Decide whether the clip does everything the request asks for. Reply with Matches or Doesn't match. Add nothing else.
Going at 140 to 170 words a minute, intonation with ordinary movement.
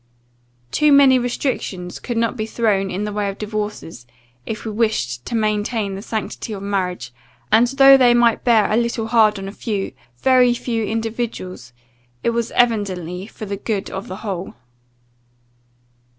Matches